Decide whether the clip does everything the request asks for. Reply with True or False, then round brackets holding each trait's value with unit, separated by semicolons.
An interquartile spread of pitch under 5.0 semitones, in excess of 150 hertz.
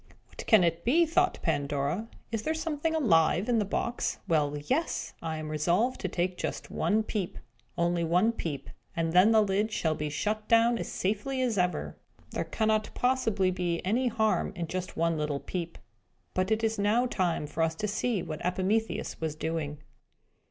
False (5.4 semitones; 185 Hz)